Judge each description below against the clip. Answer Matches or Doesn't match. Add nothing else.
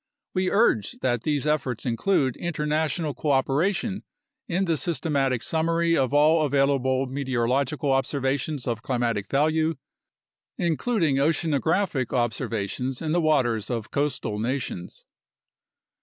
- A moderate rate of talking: Doesn't match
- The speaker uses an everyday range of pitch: Matches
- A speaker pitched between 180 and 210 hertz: Doesn't match